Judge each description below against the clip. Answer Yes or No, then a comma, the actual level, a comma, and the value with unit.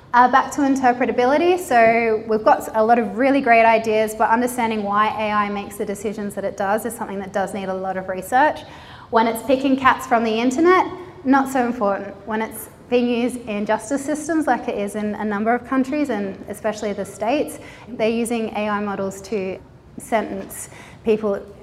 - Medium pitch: No, high, 225 Hz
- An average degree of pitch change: Yes, average, 3.1 semitones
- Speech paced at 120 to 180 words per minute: No, average, 190 wpm